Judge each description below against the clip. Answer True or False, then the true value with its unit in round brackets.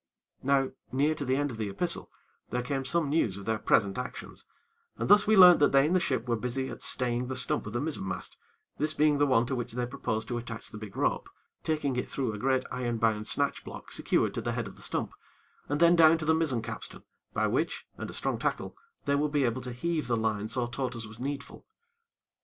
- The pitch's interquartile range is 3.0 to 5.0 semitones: True (4.1 semitones)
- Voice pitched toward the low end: True (130 Hz)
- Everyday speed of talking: False (240 wpm)